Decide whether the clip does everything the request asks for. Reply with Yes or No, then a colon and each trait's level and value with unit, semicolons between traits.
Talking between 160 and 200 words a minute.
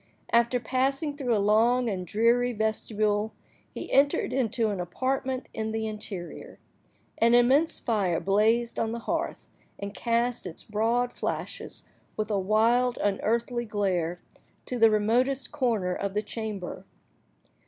No: slow, 135 wpm